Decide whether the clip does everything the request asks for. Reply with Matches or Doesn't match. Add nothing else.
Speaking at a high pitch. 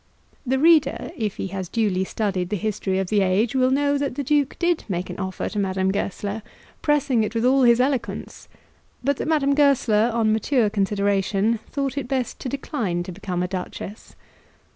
Matches